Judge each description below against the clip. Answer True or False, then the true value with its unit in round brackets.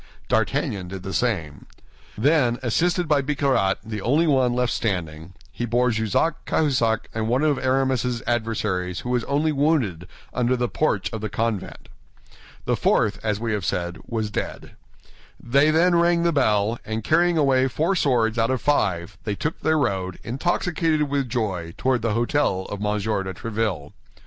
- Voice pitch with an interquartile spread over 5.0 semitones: True (5.4 semitones)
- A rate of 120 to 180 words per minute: True (165 wpm)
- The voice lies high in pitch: False (120 Hz)